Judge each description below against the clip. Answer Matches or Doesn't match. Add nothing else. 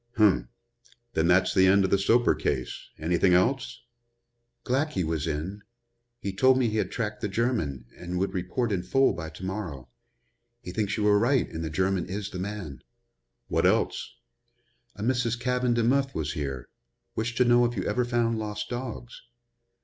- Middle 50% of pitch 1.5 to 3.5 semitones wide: Doesn't match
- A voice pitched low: Matches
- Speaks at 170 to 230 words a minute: Matches